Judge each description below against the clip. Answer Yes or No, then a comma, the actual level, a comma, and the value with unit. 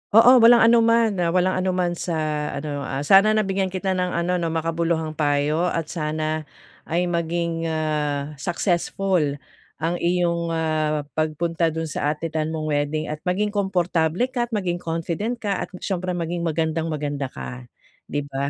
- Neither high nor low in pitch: Yes, medium, 165 Hz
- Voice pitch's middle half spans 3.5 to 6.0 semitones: No, average, 2.9 semitones